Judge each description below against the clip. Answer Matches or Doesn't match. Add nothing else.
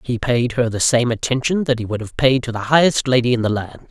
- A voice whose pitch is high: Doesn't match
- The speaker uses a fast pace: Matches